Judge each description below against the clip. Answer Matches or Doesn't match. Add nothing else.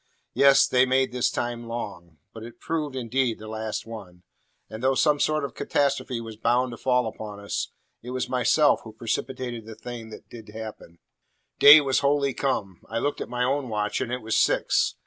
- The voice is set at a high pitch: Doesn't match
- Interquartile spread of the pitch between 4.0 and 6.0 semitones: Doesn't match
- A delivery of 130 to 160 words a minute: Doesn't match